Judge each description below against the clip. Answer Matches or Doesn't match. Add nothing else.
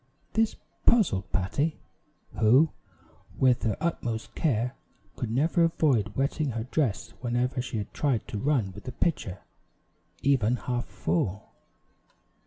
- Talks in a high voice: Doesn't match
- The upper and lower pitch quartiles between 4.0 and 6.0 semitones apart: Matches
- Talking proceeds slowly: Matches